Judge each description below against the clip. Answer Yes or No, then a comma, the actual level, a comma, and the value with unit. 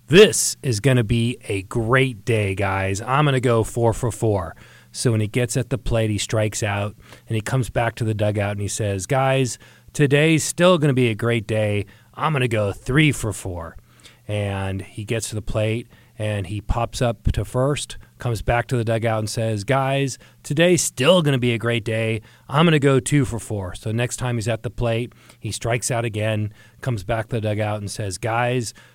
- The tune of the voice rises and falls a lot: No, average, 2.9 semitones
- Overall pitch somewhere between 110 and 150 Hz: Yes, low, 115 Hz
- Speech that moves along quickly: Yes, fast, 220 wpm